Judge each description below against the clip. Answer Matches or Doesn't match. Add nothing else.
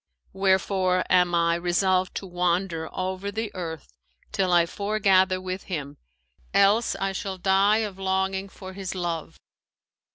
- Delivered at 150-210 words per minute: Doesn't match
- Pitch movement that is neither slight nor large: Doesn't match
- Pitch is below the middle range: Doesn't match